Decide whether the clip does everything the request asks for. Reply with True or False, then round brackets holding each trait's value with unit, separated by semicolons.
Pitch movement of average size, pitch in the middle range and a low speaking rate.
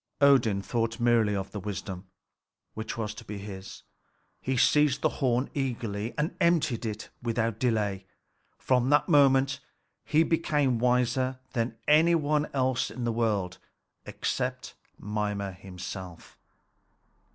False (4.3 semitones; 120 Hz; 130 wpm)